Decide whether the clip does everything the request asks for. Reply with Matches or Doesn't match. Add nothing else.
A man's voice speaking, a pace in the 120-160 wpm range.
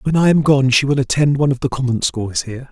Doesn't match